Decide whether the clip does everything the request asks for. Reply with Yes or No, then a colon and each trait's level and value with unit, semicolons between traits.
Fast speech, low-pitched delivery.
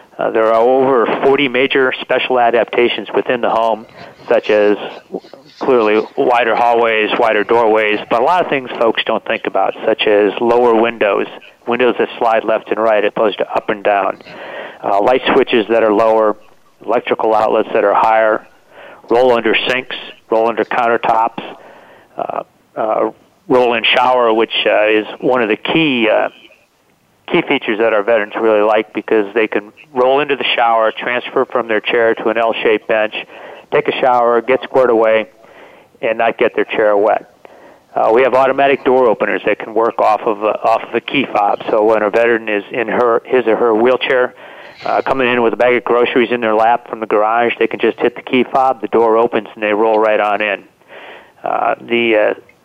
No: average, 190 wpm; low, 115 Hz